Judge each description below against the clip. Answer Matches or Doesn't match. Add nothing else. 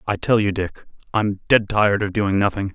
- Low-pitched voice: Matches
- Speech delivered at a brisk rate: Matches